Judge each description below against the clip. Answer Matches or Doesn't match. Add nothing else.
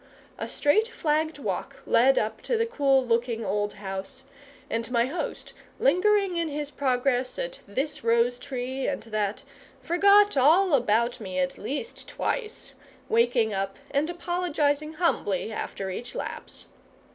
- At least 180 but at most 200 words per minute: Doesn't match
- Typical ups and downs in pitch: Doesn't match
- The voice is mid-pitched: Doesn't match